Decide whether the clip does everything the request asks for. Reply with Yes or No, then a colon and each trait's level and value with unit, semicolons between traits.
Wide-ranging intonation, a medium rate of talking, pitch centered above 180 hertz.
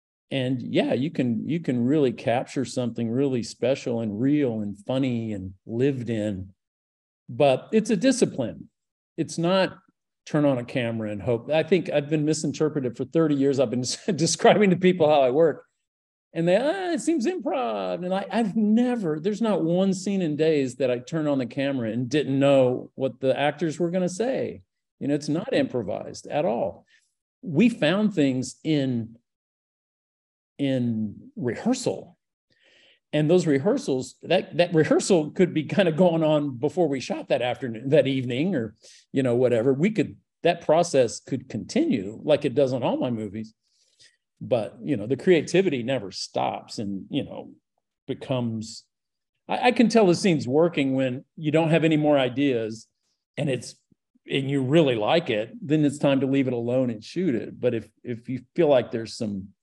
No: wide, 5.7 semitones; average, 180 wpm; medium, 140 Hz